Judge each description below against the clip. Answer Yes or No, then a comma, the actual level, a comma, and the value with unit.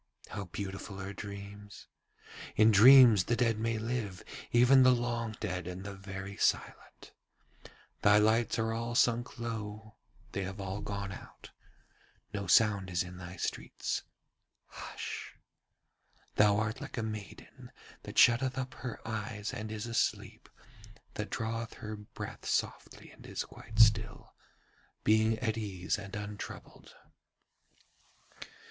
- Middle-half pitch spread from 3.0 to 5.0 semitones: No, narrow, 2.4 semitones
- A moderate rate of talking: No, slow, 130 wpm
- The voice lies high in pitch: No, low, 110 Hz